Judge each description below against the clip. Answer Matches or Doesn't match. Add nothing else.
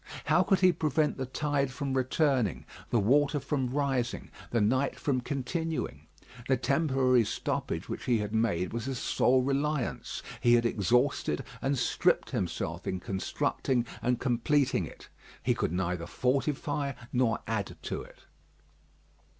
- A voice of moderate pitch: Doesn't match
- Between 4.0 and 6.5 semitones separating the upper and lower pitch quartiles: Doesn't match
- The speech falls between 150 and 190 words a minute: Doesn't match